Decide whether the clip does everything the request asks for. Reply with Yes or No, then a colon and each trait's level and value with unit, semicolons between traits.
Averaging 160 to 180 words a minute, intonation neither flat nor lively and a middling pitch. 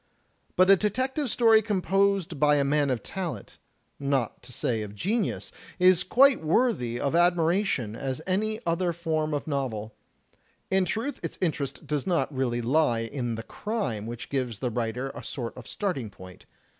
No: average, 170 wpm; wide, 7.8 semitones; medium, 150 Hz